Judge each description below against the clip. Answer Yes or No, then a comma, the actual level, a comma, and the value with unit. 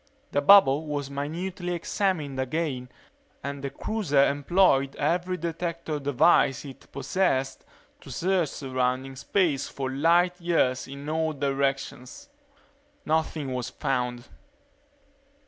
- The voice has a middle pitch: Yes, medium, 145 Hz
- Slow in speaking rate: Yes, slow, 110 wpm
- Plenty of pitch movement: No, average, 4.0 semitones